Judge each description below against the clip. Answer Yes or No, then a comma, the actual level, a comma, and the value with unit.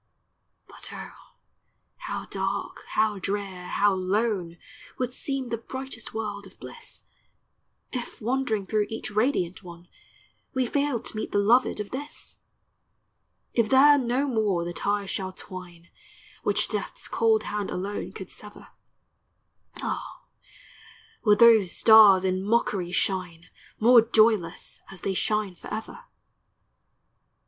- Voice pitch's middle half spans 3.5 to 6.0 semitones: Yes, average, 3.8 semitones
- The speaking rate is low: Yes, slow, 125 wpm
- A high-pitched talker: Yes, high, 210 Hz